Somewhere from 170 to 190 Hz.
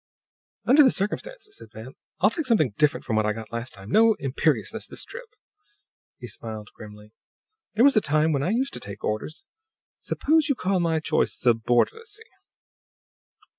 No: medium, 155 Hz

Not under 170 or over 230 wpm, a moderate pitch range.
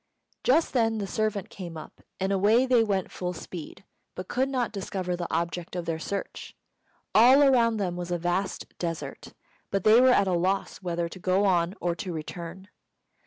Yes: average, 185 wpm; average, 3.8 semitones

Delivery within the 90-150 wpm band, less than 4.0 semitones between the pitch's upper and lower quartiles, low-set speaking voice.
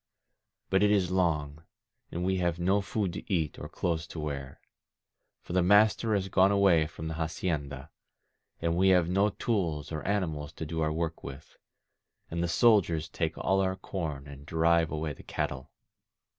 No: average, 175 wpm; average, 3.6 semitones; very low, 85 Hz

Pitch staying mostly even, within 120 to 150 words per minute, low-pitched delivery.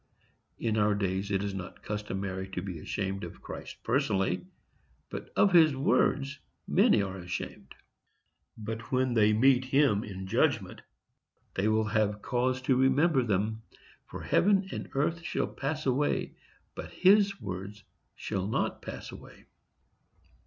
No: wide, 5.6 semitones; average, 140 wpm; low, 110 Hz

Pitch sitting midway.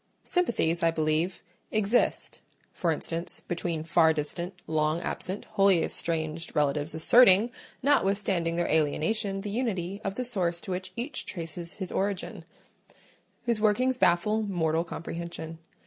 Yes: medium, 175 Hz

